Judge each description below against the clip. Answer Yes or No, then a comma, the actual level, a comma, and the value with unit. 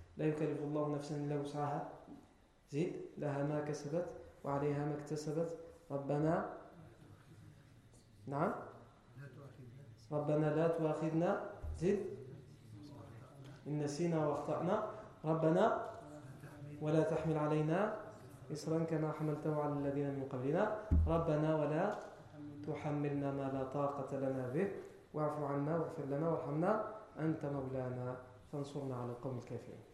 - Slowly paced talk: Yes, slow, 105 wpm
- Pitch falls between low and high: Yes, medium, 145 Hz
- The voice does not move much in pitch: Yes, narrow, 2.3 semitones